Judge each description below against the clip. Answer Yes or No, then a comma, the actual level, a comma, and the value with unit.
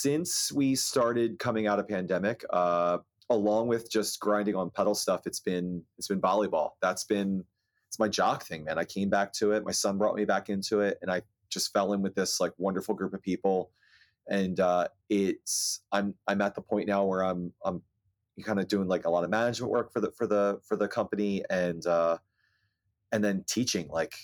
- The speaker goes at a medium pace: No, fast, 210 wpm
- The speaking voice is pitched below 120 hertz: Yes, low, 100 Hz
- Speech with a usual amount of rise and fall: No, narrow, 2.1 semitones